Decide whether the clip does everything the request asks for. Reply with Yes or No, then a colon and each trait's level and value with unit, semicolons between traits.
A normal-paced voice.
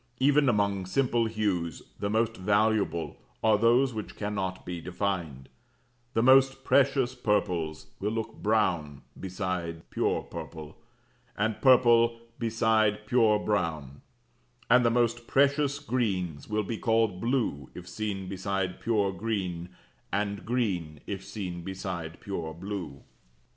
No: slow, 125 wpm